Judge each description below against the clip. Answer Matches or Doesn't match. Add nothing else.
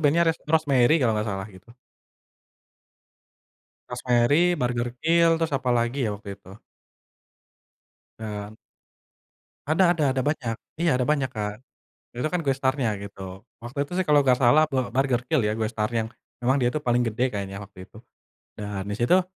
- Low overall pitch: Matches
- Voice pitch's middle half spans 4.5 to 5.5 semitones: Matches